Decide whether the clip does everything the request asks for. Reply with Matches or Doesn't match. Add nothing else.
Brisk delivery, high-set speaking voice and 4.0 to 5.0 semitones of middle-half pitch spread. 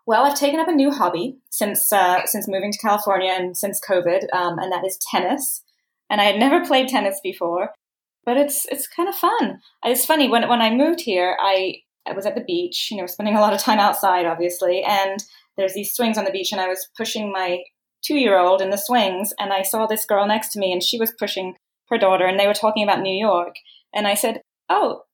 Matches